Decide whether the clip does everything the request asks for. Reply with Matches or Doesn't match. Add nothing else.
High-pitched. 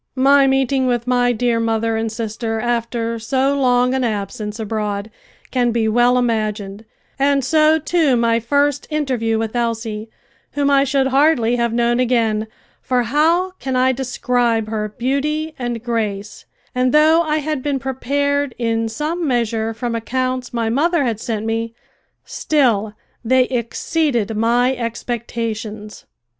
Matches